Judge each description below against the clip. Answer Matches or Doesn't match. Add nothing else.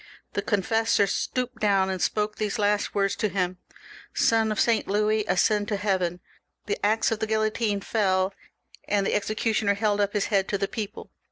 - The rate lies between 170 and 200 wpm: Matches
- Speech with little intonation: Matches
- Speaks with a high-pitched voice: Matches